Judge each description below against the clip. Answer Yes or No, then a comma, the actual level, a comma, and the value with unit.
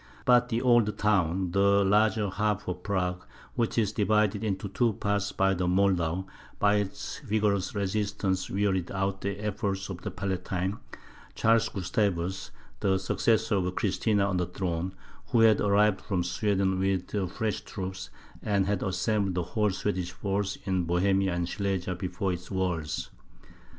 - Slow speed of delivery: No, average, 150 wpm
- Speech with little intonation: Yes, narrow, 2.0 semitones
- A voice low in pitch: Yes, very low, 95 Hz